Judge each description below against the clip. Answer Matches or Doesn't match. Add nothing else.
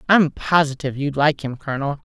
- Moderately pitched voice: Matches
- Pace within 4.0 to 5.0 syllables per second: Doesn't match